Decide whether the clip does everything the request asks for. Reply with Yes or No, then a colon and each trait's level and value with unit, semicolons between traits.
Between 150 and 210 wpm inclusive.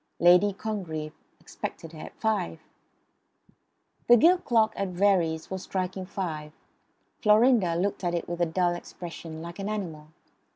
No: average, 140 wpm